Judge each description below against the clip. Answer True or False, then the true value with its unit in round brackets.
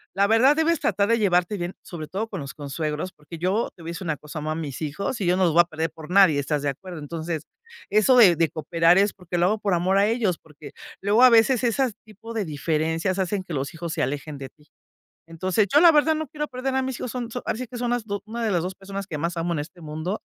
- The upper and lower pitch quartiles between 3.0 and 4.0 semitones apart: False (5.5 semitones)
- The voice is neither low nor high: True (180 Hz)